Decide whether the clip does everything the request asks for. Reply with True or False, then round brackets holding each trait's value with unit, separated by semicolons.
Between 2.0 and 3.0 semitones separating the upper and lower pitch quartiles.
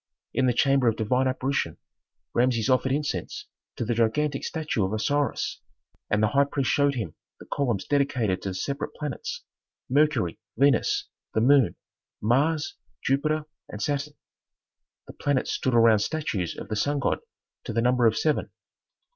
False (4.3 semitones)